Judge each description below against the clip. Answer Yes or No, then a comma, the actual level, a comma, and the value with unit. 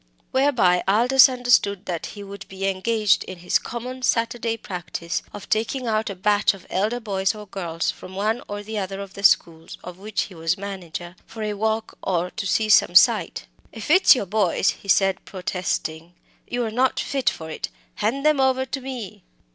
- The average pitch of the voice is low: No, high, 205 Hz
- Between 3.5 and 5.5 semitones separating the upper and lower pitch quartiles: Yes, average, 3.8 semitones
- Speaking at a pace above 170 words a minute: Yes, average, 185 wpm